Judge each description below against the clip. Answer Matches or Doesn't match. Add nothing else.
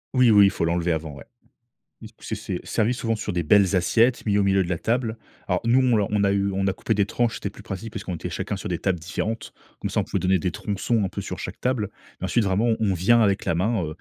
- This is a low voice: Matches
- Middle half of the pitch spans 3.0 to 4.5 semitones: Matches